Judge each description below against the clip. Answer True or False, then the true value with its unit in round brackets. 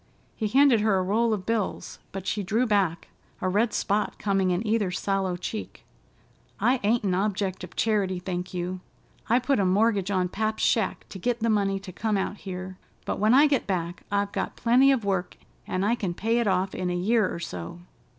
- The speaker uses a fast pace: True (210 wpm)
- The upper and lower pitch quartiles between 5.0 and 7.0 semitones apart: False (3.2 semitones)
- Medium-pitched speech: False (200 Hz)